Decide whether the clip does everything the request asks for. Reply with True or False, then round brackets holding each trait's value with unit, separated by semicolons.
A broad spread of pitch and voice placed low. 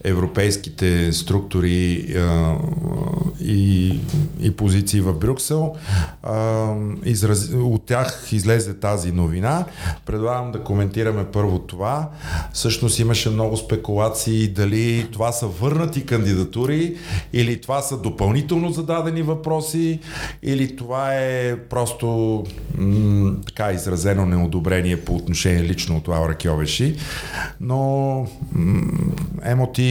True (5.7 semitones; 110 Hz)